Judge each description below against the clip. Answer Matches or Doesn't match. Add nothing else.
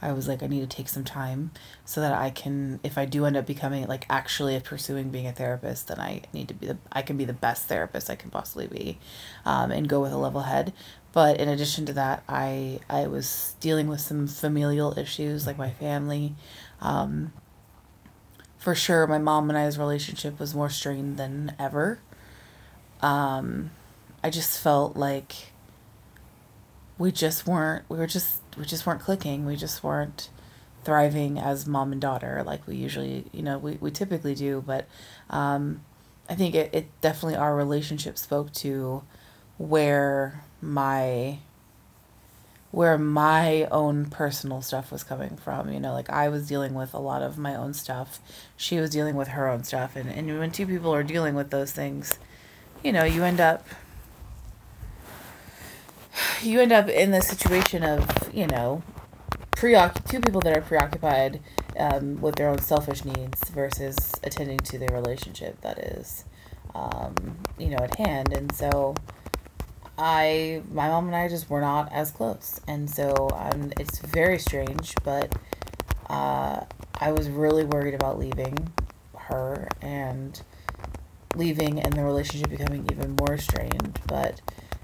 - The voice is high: Doesn't match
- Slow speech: Doesn't match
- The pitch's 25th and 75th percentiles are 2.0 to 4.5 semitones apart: Matches